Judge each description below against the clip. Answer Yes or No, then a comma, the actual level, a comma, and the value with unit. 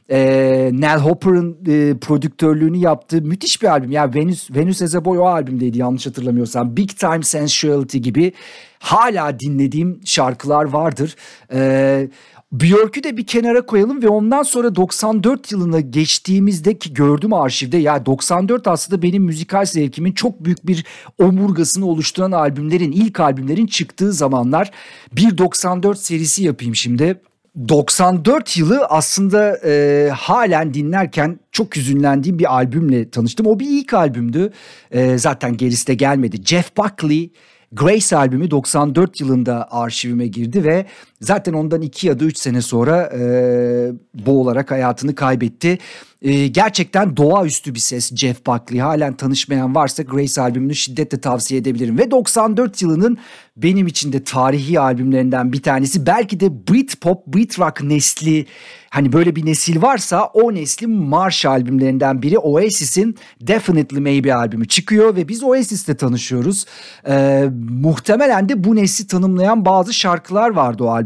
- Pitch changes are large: Yes, wide, 5.9 semitones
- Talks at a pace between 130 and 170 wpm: Yes, fast, 140 wpm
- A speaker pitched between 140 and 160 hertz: Yes, medium, 155 Hz